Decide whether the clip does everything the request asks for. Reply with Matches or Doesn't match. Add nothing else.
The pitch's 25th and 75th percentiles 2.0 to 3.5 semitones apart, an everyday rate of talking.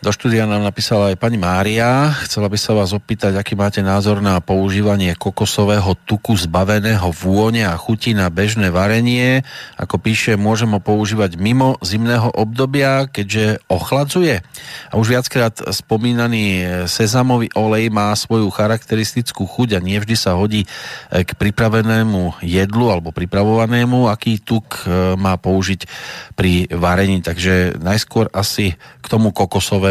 Matches